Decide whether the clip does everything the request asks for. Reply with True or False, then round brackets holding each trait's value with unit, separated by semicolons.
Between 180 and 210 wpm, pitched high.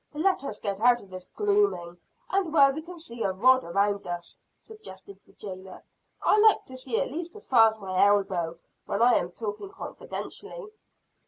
True (185 wpm; 225 Hz)